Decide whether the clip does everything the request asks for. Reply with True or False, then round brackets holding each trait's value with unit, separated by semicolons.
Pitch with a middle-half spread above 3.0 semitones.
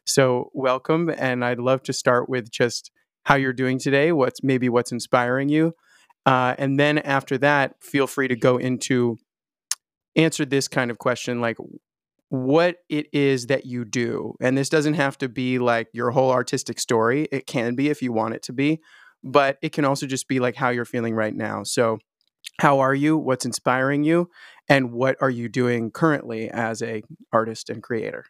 False (2.4 semitones)